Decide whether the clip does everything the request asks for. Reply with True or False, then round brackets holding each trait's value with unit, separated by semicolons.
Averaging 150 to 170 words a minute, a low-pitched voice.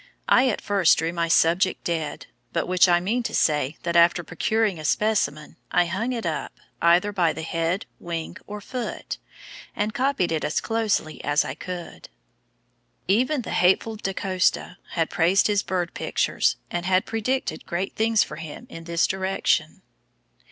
False (165 wpm; 180 Hz)